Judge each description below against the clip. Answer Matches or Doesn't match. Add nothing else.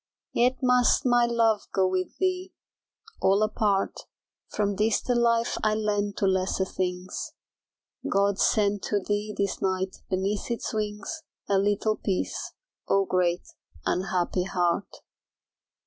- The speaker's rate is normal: Doesn't match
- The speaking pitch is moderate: Doesn't match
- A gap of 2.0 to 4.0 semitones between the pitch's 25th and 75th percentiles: Matches